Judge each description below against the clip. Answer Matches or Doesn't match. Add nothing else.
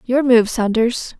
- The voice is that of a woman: Matches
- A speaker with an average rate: Matches